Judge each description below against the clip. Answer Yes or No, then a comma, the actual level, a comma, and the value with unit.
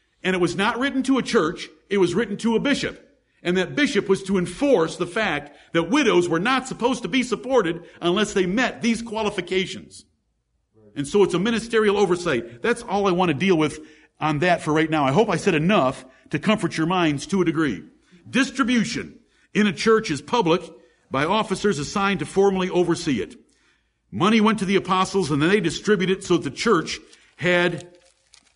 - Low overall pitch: No, medium, 185 Hz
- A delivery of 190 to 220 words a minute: Yes, average, 195 wpm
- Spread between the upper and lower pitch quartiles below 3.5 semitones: No, average, 4.2 semitones